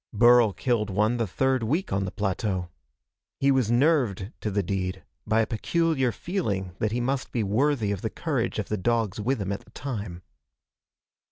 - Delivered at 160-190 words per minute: Yes, average, 185 wpm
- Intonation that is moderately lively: Yes, average, 4.5 semitones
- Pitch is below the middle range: Yes, low, 110 Hz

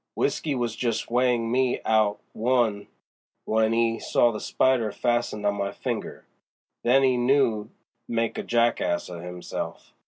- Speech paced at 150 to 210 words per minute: Yes, average, 155 wpm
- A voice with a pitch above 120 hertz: No, low, 115 Hz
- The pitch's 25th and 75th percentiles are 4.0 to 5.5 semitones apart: No, narrow, 2.4 semitones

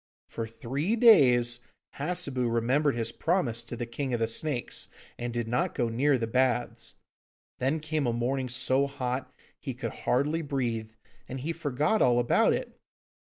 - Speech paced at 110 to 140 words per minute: No, average, 160 wpm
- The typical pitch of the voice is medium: No, low, 130 Hz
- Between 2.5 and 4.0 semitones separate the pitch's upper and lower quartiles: Yes, average, 3.4 semitones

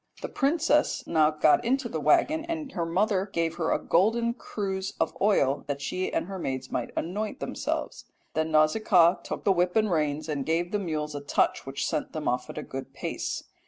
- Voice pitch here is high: No, medium, 170 Hz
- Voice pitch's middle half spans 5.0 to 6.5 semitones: Yes, wide, 5.6 semitones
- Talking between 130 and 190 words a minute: No, average, 200 wpm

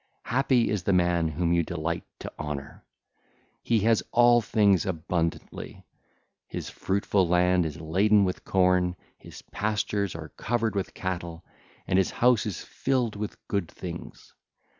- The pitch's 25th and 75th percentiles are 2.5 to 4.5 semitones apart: Yes, average, 3.8 semitones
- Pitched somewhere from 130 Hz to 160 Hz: No, very low, 95 Hz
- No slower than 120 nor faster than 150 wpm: Yes, average, 140 wpm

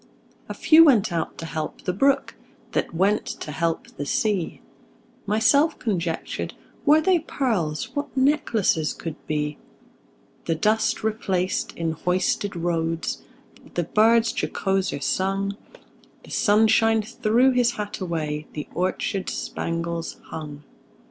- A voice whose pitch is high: Yes, high, 195 Hz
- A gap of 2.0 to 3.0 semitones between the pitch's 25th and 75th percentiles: No, average, 5.2 semitones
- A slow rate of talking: Yes, slow, 120 wpm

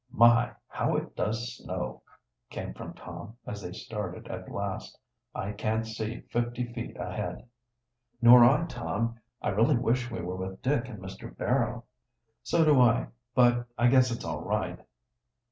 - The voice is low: Yes, low, 120 Hz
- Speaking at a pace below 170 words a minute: Yes, average, 160 wpm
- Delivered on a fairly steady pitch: Yes, narrow, 2.2 semitones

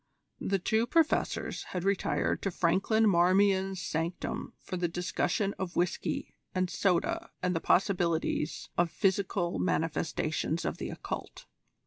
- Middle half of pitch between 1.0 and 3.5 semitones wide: Yes, narrow, 2.6 semitones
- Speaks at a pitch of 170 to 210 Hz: Yes, medium, 185 Hz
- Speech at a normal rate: No, slow, 125 wpm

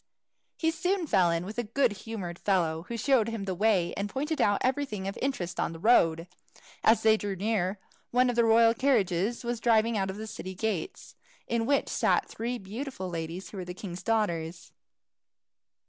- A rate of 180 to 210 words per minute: Yes, average, 190 wpm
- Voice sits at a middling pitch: No, high, 215 Hz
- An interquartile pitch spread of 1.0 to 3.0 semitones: No, average, 4.4 semitones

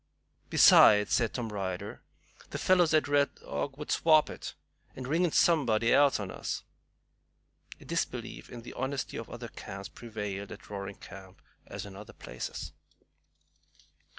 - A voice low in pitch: Yes, low, 115 Hz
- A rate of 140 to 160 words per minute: Yes, average, 150 wpm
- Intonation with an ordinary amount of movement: No, wide, 6.0 semitones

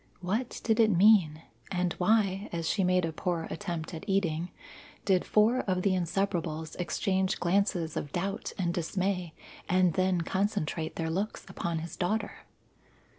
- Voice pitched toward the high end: No, medium, 180 Hz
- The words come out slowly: No, average, 150 wpm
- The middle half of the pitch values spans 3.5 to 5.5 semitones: No, average, 2.9 semitones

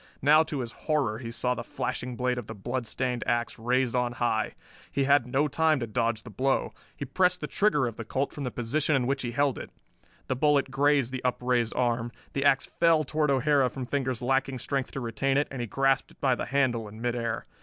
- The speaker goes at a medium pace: No, fast, 225 wpm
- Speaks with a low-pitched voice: Yes, low, 130 Hz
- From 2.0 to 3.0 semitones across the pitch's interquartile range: Yes, narrow, 2.6 semitones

